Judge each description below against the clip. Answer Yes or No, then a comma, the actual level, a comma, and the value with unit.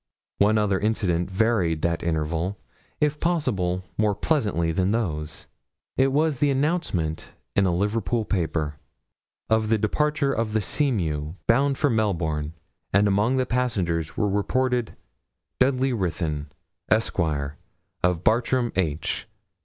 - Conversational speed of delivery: No, slow, 125 wpm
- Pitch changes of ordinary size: No, wide, 6.7 semitones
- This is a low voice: Yes, low, 105 Hz